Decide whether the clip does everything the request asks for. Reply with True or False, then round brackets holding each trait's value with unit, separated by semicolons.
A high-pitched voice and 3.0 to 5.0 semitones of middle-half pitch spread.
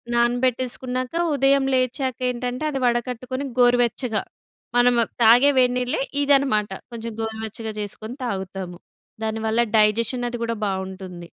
False (240 Hz; 2.5 semitones)